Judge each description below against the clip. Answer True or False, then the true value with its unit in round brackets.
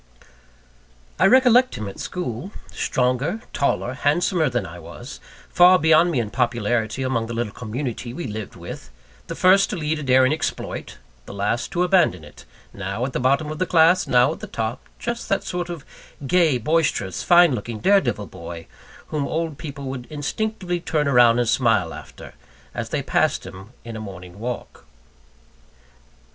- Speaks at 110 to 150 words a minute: False (175 wpm)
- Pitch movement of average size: False (6.9 semitones)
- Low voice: True (130 Hz)